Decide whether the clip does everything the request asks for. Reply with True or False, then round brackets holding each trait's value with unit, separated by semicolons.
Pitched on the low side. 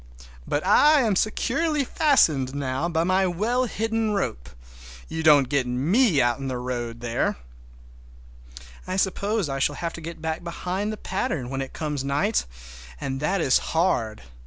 False (160 Hz)